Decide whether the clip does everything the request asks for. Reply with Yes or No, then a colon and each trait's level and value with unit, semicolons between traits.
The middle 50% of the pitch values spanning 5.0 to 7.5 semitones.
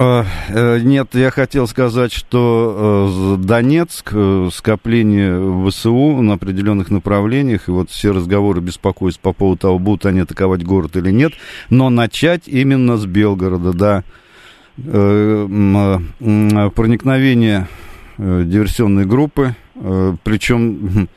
No: average, 3.8 semitones